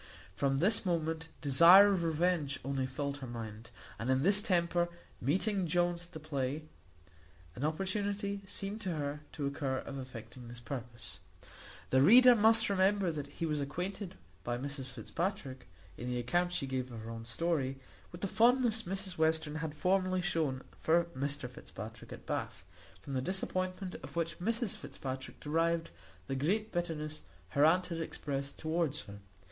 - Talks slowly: No, average, 165 wpm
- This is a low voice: No, medium, 160 Hz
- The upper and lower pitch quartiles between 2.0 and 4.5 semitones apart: No, wide, 5.4 semitones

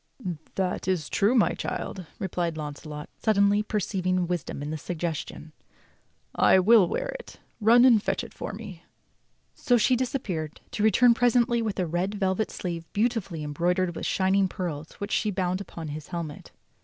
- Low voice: No, medium, 185 Hz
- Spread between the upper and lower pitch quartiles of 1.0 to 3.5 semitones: No, average, 4.3 semitones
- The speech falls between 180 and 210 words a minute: No, average, 160 wpm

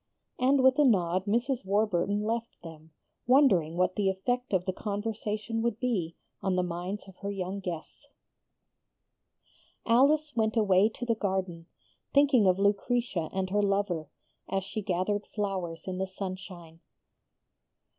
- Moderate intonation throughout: Yes, average, 3.7 semitones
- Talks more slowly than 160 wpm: Yes, average, 145 wpm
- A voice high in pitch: Yes, high, 200 Hz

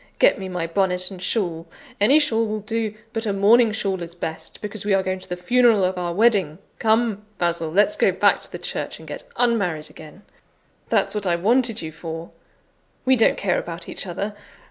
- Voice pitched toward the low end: No, high, 195 Hz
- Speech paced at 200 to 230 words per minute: Yes, fast, 205 wpm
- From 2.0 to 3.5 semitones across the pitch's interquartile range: No, average, 4.2 semitones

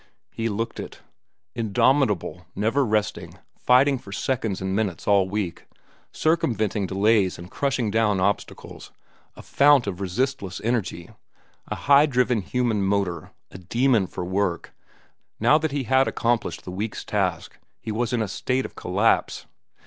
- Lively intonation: No, average, 4.7 semitones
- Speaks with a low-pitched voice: Yes, low, 110 Hz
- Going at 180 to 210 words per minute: No, average, 145 wpm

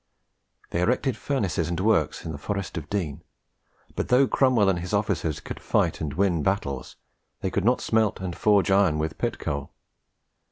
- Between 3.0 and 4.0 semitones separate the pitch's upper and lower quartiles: No, average, 4.8 semitones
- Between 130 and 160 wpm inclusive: No, average, 175 wpm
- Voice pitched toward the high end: No, very low, 95 Hz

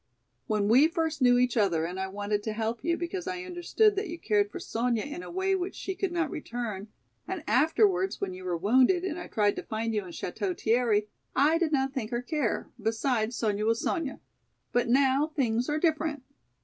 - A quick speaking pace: Yes, fast, 210 wpm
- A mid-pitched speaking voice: No, very high, 250 Hz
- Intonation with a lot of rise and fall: Yes, wide, 7.2 semitones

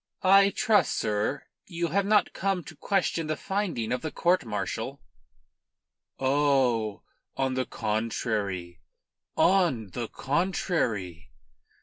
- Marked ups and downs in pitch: Yes, wide, 8.8 semitones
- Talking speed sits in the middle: No, slow, 110 wpm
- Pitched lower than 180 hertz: Yes, low, 135 Hz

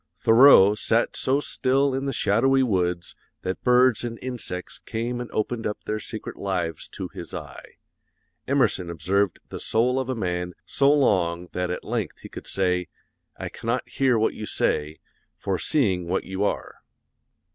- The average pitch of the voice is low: Yes, low, 110 Hz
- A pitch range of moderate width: No, wide, 5.9 semitones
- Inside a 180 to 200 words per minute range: No, average, 165 wpm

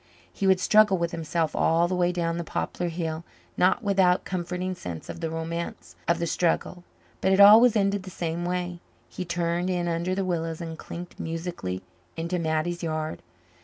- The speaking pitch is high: No, medium, 175 Hz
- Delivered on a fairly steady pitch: Yes, narrow, 1.8 semitones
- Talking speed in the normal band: Yes, average, 185 wpm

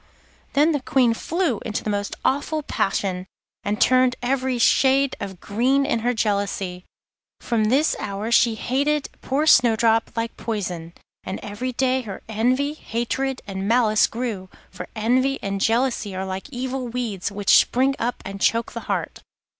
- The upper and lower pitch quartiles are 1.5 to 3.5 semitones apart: No, average, 4.3 semitones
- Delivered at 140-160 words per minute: Yes, average, 155 wpm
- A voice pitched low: No, high, 235 Hz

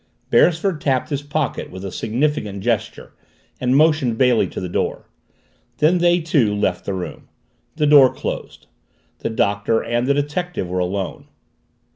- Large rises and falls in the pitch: Yes, wide, 6.9 semitones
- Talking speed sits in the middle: Yes, average, 150 wpm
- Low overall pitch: Yes, low, 130 Hz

